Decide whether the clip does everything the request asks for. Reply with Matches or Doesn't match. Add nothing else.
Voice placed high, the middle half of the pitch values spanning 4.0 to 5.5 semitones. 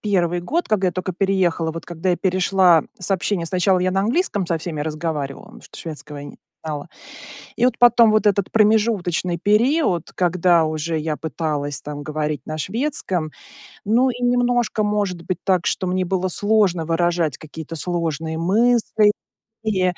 Doesn't match